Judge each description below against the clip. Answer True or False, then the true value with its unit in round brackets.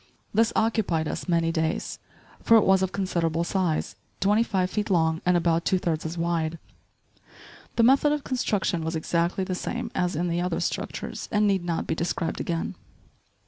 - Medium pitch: True (175 Hz)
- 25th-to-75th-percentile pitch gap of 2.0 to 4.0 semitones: True (3.1 semitones)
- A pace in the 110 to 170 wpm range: False (180 wpm)